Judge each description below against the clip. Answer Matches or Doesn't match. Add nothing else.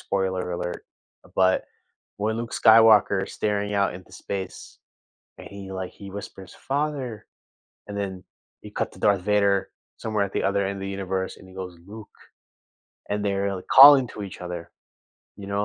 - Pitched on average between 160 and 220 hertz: Doesn't match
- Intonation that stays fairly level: Matches